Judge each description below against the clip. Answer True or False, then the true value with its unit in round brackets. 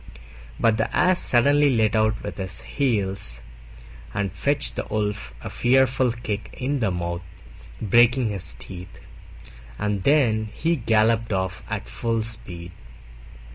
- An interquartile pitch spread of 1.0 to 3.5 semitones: False (4.3 semitones)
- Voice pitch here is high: False (110 Hz)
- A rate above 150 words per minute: False (135 wpm)